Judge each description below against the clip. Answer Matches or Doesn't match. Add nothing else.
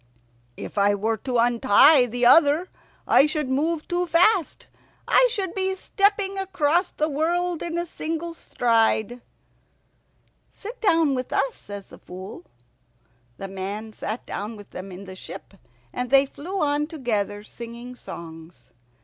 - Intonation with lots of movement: Matches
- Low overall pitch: Doesn't match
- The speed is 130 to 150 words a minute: Matches